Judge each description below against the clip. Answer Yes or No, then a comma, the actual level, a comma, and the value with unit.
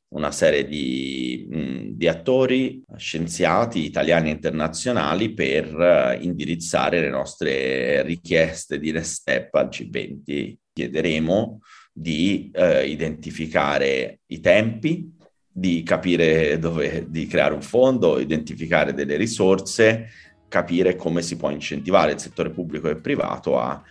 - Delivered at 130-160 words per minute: No, slow, 115 wpm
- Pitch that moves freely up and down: No, average, 4.5 semitones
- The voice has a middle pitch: No, very low, 85 Hz